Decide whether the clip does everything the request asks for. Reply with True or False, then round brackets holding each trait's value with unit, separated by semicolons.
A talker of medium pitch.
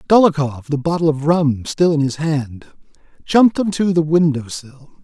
True (155 Hz)